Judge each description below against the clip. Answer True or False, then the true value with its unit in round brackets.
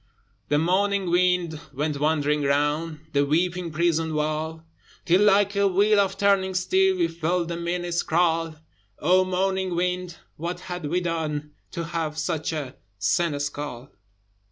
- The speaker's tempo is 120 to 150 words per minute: True (140 wpm)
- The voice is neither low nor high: True (170 Hz)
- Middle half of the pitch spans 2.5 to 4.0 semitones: True (3.0 semitones)